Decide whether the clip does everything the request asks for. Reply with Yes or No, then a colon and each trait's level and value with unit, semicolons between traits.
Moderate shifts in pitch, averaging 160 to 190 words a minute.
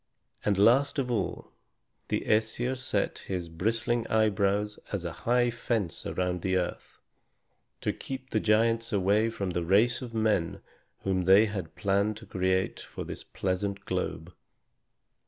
No: average, 3.5 semitones; average, 145 wpm